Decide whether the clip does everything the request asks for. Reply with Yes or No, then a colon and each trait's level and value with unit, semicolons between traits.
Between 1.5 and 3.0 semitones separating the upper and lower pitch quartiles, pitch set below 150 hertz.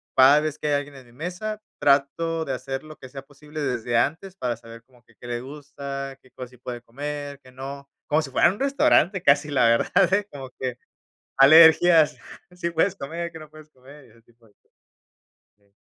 No: average, 3.8 semitones; medium, 140 Hz